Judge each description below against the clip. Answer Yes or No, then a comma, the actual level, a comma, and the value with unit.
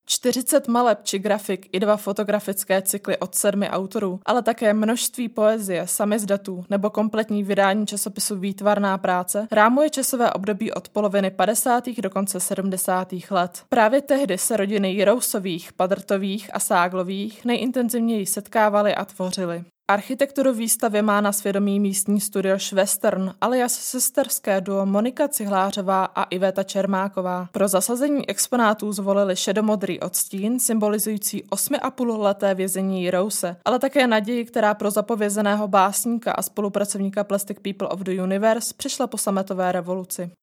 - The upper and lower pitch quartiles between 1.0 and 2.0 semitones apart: No, narrow, 2.4 semitones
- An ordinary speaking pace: Yes, average, 130 wpm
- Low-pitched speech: No, high, 205 Hz